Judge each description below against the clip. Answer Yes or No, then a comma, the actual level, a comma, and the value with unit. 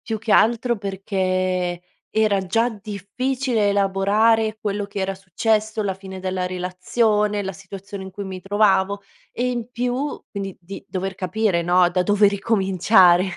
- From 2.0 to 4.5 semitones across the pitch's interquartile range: Yes, narrow, 2.5 semitones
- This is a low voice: No, high, 200 Hz